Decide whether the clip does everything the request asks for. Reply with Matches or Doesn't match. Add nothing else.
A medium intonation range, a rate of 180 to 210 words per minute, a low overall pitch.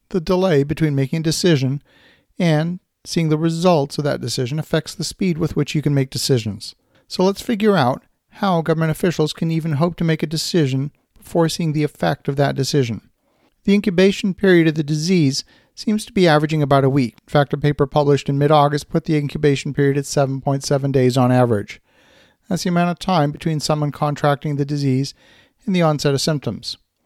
Doesn't match